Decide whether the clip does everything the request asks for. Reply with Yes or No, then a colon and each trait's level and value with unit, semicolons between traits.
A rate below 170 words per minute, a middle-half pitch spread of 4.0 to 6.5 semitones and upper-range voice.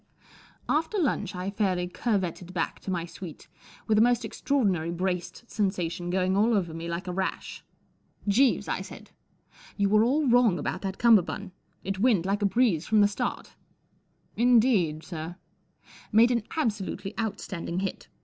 No: average, 180 wpm; average, 4.4 semitones; high, 195 Hz